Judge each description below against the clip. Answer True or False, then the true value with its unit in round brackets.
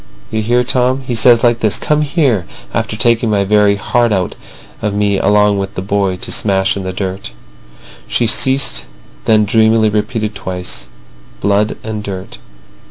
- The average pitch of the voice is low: True (105 Hz)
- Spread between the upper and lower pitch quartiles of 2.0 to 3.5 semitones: True (2.9 semitones)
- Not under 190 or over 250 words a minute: False (165 wpm)